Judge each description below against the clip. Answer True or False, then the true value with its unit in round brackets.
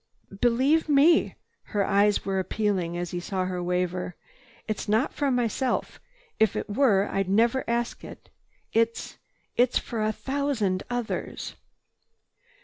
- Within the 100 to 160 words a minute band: True (135 wpm)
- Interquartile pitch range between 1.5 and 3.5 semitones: False (4.4 semitones)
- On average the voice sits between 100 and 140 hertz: False (215 Hz)